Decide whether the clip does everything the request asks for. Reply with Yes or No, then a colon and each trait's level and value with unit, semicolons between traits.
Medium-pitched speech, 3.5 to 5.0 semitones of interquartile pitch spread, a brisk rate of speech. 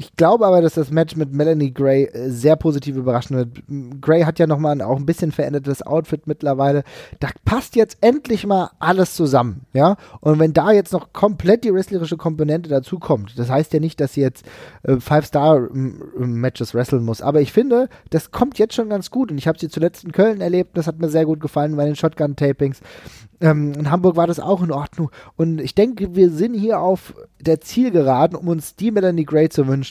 Yes: medium, 155 Hz; average, 4.2 semitones; fast, 215 wpm